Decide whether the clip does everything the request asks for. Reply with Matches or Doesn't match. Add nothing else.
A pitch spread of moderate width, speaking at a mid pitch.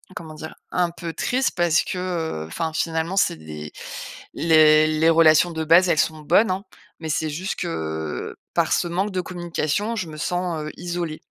Doesn't match